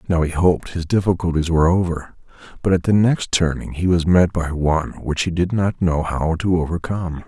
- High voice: No, very low, 85 Hz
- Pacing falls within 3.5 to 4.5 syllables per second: No, 5.4 syllables/s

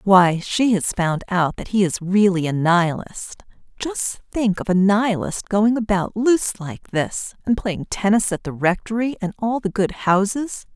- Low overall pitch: No, high, 200 Hz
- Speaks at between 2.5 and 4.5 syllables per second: Yes, 4.4 syllables/s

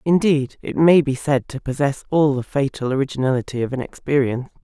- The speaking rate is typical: Yes, average, 170 wpm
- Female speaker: Yes, female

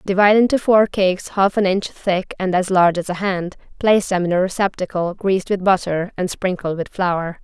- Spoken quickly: Yes, fast, 210 wpm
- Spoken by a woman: Yes, female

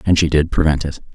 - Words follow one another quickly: Yes, fast, 260 wpm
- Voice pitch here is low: Yes, very low, 75 Hz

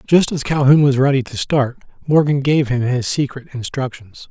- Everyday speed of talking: Yes, average, 180 wpm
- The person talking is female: No, male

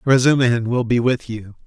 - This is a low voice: Yes, low, 120 Hz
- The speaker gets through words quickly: No, average, 180 wpm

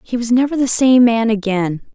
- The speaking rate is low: No, fast, 215 wpm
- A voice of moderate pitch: No, high, 235 Hz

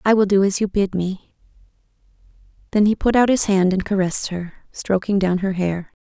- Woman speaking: Yes, female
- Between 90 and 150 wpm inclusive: No, average, 200 wpm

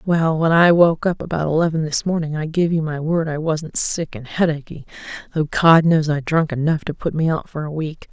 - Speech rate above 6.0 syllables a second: No, 5.2 syllables/s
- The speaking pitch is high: No, medium, 160 Hz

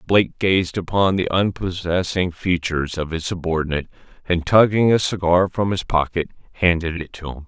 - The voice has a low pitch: Yes, very low, 90 Hz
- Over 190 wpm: No, average, 160 wpm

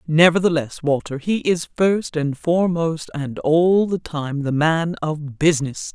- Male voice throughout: No, female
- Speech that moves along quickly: No, average, 150 wpm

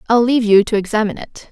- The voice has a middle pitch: No, high, 220 Hz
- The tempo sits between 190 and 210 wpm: No, fast, 240 wpm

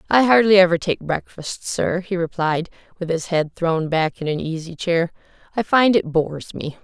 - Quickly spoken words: No, average, 195 wpm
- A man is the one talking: No, female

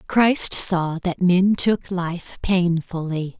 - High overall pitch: No, medium, 180 Hz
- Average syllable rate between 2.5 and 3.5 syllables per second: Yes, 2.9 syllables/s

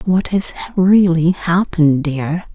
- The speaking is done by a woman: Yes, female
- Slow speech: Yes, slow, 120 wpm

